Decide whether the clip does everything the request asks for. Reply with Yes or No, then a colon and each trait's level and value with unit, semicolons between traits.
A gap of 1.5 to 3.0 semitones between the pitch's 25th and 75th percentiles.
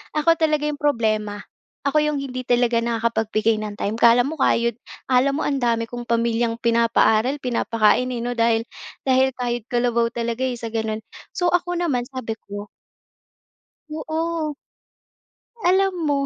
No: average, 3.6 semitones